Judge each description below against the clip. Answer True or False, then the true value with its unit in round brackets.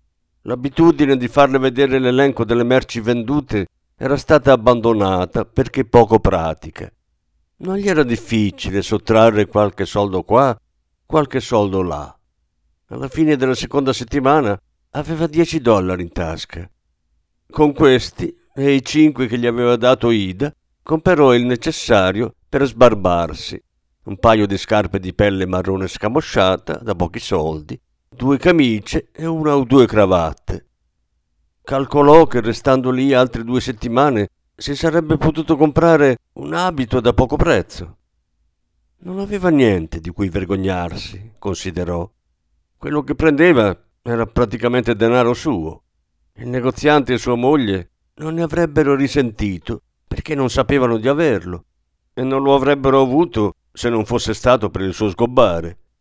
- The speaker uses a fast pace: False (135 wpm)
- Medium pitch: False (115 Hz)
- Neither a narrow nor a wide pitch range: False (7.1 semitones)